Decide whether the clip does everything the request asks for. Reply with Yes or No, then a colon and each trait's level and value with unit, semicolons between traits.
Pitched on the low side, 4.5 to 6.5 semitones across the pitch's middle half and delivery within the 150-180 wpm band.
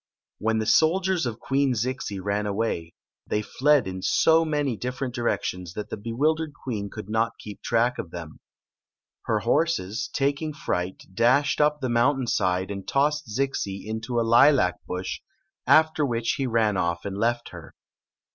Yes: low, 120 Hz; wide, 5.6 semitones; average, 165 wpm